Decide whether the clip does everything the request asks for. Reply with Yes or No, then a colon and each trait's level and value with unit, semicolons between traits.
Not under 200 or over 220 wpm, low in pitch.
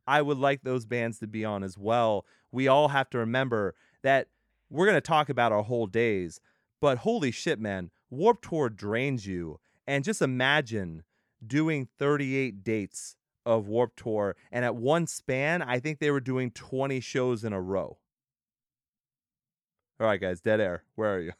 No: average, 175 wpm; low, 120 Hz